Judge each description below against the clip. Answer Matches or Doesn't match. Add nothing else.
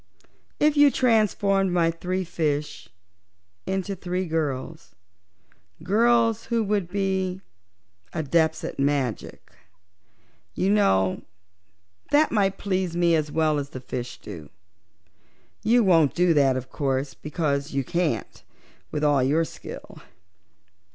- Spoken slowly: Matches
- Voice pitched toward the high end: Doesn't match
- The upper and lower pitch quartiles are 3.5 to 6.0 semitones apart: Matches